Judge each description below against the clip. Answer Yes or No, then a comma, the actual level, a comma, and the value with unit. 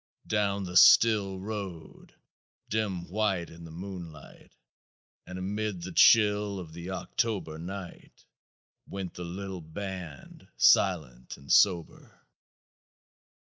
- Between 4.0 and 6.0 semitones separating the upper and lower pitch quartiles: No, average, 2.9 semitones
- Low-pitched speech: Yes, very low, 95 Hz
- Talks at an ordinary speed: No, slow, 105 wpm